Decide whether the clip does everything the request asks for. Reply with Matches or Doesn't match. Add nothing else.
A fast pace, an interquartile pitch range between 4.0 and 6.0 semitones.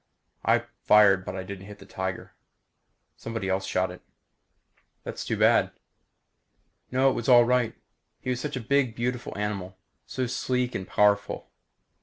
Doesn't match